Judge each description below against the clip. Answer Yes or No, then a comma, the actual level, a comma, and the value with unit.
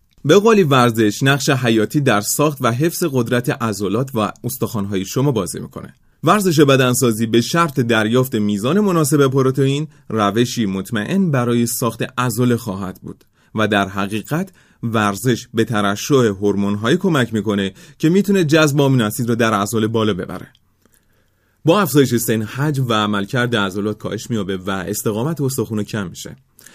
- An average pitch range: Yes, average, 4.8 semitones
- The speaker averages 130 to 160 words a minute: Yes, average, 140 wpm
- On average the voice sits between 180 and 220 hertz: No, low, 120 Hz